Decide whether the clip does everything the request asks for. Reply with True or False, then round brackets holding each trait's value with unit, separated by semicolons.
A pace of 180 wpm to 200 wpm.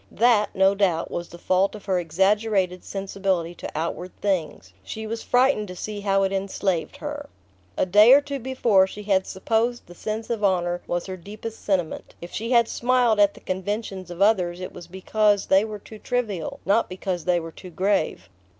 True (195 wpm)